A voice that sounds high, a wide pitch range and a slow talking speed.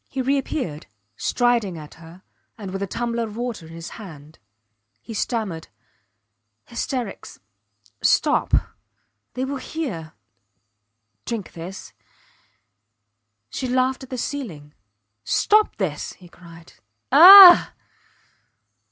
Yes: high, 220 Hz; wide, 7.5 semitones; slow, 105 wpm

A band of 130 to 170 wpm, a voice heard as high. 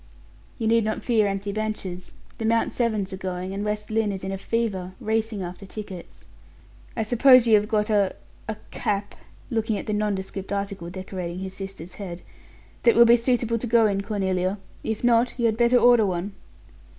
No: average, 185 wpm; high, 210 Hz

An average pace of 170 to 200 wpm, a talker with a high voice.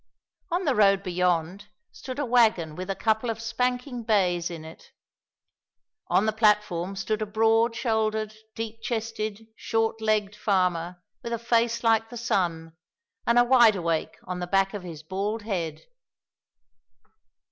No: average, 150 wpm; high, 215 Hz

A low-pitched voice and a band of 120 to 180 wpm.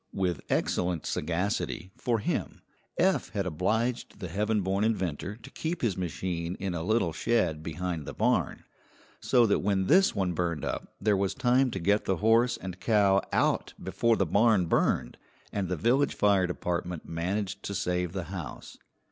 Yes: very low, 95 Hz; average, 170 wpm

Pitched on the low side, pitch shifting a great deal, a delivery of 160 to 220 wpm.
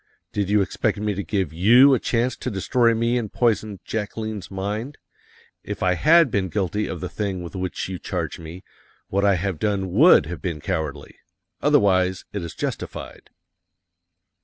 No: low, 100 Hz; average, 3.1 semitones; average, 170 wpm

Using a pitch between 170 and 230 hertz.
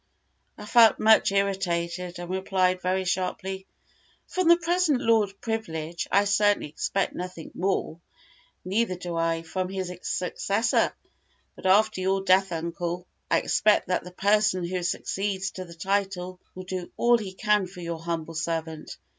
Yes: medium, 185 Hz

